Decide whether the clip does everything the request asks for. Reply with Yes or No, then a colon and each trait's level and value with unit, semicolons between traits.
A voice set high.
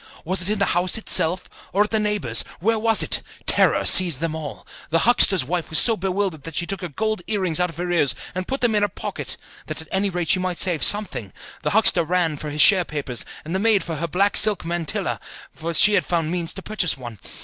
No: medium, 180 Hz